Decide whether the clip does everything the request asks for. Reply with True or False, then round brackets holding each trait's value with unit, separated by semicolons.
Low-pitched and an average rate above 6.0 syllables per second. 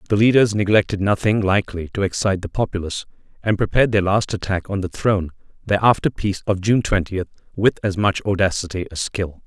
True (100 Hz; 6.2 syllables/s)